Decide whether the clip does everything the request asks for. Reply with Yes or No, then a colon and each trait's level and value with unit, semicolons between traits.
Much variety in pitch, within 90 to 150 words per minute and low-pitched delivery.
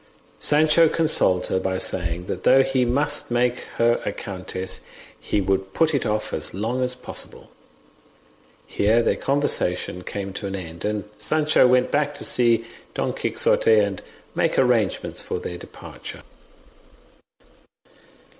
Yes: wide, 7.3 semitones; average, 140 wpm; low, 120 Hz